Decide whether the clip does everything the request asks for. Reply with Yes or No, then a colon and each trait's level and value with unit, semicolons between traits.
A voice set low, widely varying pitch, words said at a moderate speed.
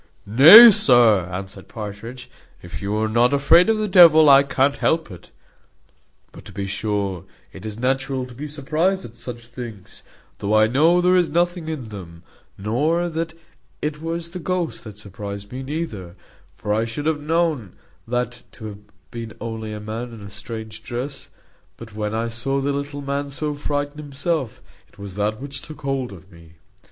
Yes: low, 125 Hz; wide, 6.0 semitones; average, 180 wpm